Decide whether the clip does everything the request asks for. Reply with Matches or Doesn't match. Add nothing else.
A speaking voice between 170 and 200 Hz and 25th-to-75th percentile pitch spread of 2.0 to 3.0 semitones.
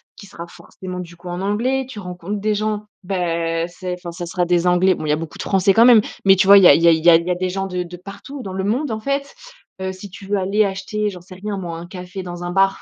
Matches